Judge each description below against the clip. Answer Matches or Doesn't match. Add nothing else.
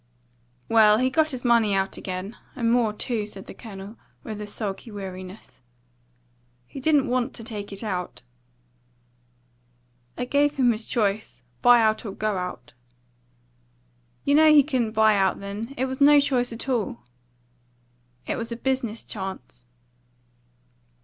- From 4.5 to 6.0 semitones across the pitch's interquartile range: Doesn't match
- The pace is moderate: Matches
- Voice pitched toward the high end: Matches